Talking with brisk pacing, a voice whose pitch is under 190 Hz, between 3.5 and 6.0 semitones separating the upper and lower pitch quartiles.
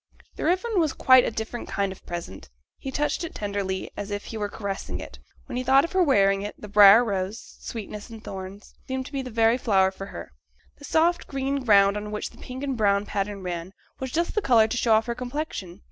No: fast, 230 wpm; high, 220 Hz; average, 4.9 semitones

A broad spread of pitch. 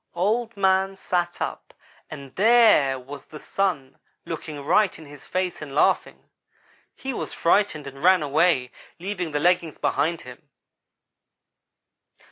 No: average, 4.8 semitones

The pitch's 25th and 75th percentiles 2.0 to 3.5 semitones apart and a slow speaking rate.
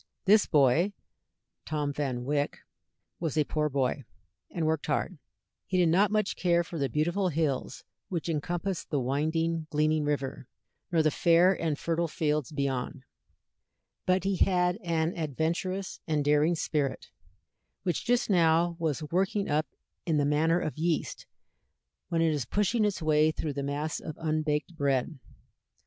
No: average, 2.8 semitones; average, 150 wpm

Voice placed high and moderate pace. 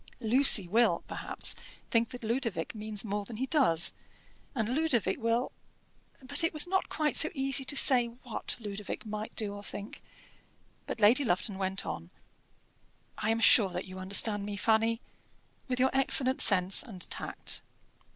Yes: high, 225 Hz; average, 160 wpm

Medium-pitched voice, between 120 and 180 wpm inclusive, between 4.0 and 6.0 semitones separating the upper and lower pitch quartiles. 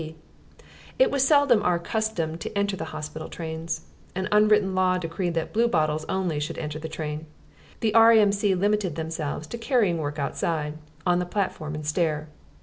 Yes: medium, 170 Hz; average, 165 wpm; average, 4.8 semitones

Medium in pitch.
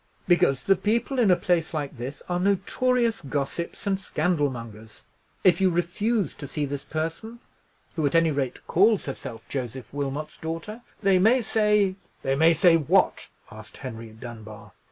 Yes: medium, 165 Hz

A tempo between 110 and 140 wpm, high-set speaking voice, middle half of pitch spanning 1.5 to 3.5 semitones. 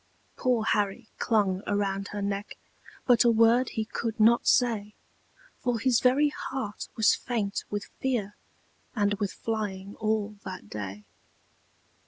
Yes: slow, 135 wpm; high, 215 Hz; average, 2.7 semitones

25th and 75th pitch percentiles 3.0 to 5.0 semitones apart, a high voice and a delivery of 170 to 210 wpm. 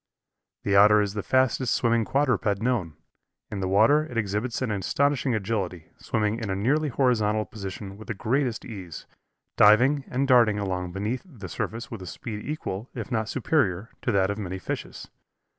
No: average, 4.1 semitones; low, 110 Hz; average, 175 wpm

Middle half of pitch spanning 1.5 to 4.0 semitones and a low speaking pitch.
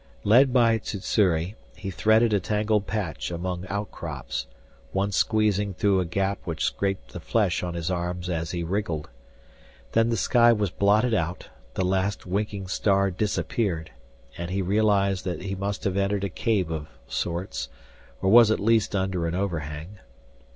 Yes: average, 2.9 semitones; very low, 95 Hz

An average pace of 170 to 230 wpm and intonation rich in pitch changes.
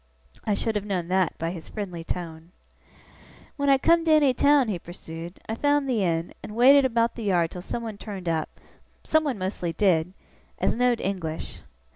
Yes: average, 180 wpm; wide, 6.3 semitones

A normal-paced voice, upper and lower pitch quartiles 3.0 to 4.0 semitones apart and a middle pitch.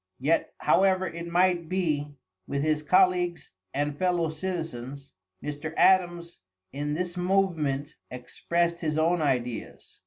No: slow, 120 wpm; average, 3.4 semitones; medium, 165 Hz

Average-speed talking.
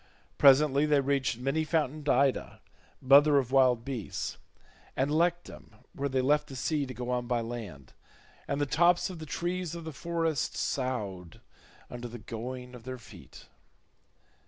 Yes: average, 160 wpm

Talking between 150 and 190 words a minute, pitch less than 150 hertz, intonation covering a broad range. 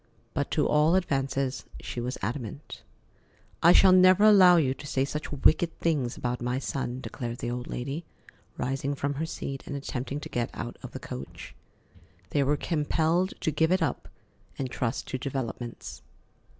No: average, 170 wpm; medium, 140 Hz; average, 4.3 semitones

